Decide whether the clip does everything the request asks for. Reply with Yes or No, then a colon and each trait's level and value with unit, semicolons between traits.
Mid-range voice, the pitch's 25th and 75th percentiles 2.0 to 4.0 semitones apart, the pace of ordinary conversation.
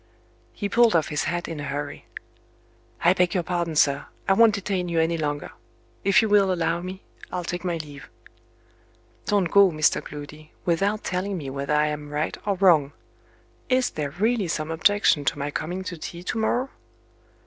No: medium, 175 Hz; average, 4.5 semitones; average, 180 wpm